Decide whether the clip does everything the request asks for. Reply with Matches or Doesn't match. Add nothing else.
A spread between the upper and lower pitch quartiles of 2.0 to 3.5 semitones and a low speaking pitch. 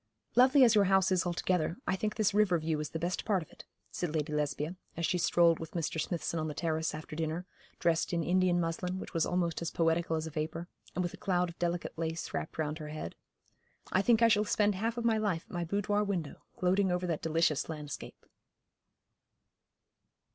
Doesn't match